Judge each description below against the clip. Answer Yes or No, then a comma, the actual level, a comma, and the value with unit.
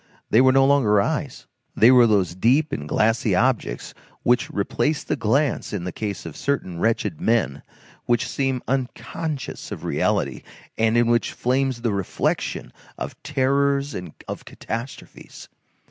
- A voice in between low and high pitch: No, low, 120 Hz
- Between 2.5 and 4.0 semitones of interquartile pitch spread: No, average, 4.5 semitones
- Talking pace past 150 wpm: No, average, 145 wpm